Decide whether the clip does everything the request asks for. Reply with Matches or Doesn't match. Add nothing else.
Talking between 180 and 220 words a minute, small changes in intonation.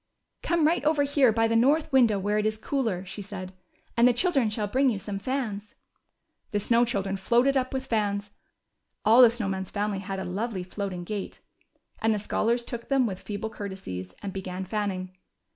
Doesn't match